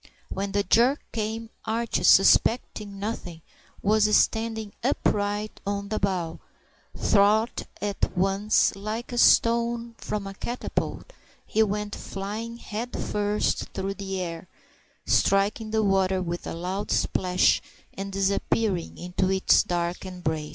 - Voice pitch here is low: No, high, 200 Hz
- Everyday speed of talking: No, slow, 130 wpm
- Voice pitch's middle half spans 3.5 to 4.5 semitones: No, narrow, 2.4 semitones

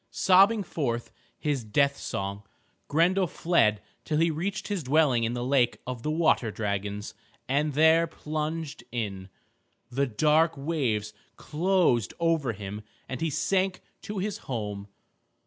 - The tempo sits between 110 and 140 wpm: Yes, slow, 135 wpm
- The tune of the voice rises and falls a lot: Yes, wide, 6.3 semitones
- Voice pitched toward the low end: No, medium, 145 Hz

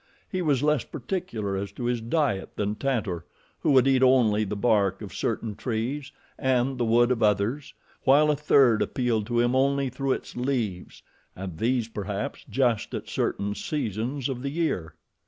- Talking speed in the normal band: Yes, average, 175 wpm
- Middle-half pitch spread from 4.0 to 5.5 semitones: Yes, average, 4.5 semitones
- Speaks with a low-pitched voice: Yes, low, 120 Hz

